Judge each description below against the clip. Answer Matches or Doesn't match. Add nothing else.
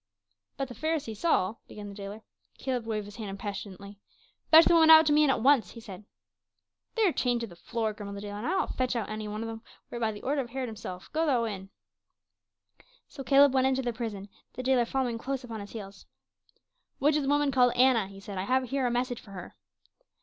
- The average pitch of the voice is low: Doesn't match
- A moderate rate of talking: Doesn't match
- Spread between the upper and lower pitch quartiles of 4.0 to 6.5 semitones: Matches